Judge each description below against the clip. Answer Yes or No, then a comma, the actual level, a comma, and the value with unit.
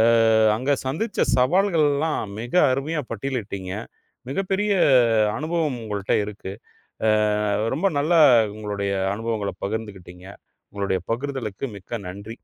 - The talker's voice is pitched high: No, low, 115 Hz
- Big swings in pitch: Yes, wide, 6.2 semitones